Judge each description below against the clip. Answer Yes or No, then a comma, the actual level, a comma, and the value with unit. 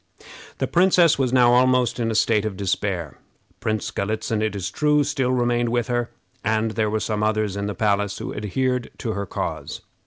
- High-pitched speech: No, low, 110 Hz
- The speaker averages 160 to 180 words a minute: No, average, 190 wpm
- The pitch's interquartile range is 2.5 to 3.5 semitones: Yes, average, 3.1 semitones